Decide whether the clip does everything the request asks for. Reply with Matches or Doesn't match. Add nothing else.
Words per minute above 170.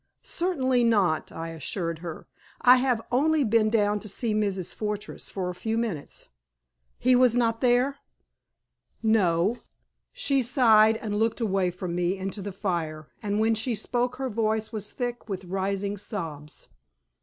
Doesn't match